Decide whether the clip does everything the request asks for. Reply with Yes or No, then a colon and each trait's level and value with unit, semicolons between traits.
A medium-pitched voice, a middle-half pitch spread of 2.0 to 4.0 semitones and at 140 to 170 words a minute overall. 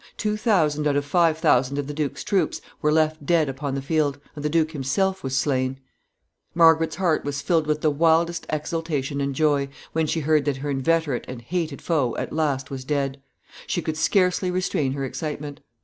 No: medium, 150 Hz; average, 2.7 semitones; average, 195 wpm